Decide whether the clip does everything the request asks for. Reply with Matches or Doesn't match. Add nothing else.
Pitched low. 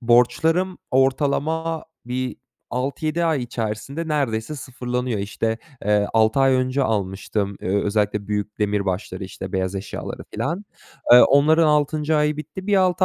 Matches